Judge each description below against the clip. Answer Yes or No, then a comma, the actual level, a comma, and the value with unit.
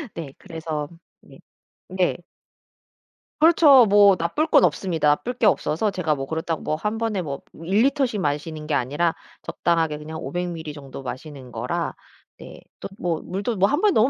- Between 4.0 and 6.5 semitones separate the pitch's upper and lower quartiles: Yes, wide, 5.4 semitones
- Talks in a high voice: No, medium, 170 Hz